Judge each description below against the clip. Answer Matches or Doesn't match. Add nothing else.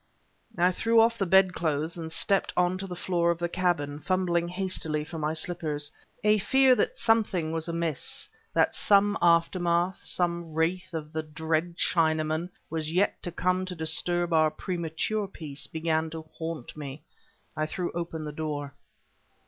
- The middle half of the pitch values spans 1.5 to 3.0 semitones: Matches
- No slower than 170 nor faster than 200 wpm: Doesn't match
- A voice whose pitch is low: Doesn't match